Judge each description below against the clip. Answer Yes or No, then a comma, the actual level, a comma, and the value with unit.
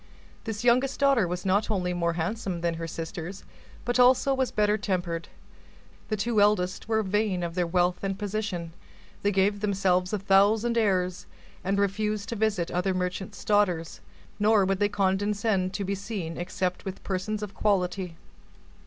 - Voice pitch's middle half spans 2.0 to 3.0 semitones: Yes, average, 2.7 semitones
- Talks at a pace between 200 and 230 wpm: No, average, 160 wpm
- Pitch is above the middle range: Yes, high, 195 Hz